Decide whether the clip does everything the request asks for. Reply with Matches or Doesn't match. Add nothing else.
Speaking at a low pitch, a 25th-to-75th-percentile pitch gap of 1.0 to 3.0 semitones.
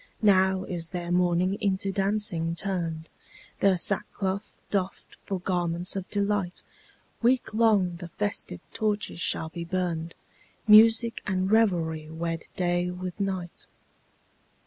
Doesn't match